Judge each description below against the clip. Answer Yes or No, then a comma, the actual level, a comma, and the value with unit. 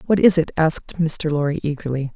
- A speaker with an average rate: Yes, average, 195 wpm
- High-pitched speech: No, medium, 155 Hz